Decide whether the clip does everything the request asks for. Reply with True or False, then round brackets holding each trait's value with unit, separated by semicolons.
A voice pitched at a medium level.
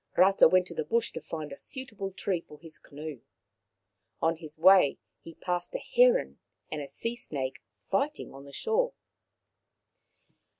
True (175 Hz)